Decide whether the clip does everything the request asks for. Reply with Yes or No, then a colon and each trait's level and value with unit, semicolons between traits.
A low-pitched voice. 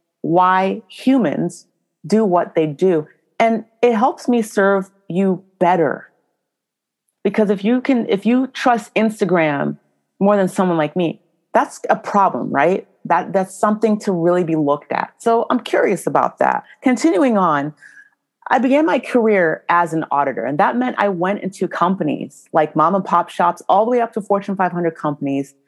No: high, 195 Hz